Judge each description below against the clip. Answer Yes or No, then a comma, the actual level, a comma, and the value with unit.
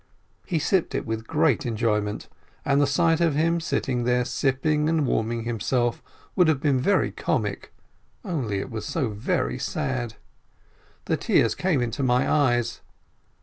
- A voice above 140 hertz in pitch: No, low, 130 Hz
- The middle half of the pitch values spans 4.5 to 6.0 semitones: Yes, average, 4.8 semitones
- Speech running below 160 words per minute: Yes, average, 150 wpm